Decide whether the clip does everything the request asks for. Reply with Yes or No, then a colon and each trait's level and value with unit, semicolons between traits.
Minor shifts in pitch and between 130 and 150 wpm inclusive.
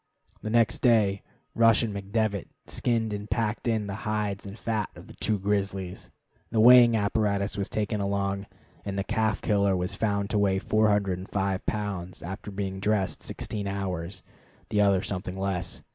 No: narrow, 1.8 semitones; average, 160 wpm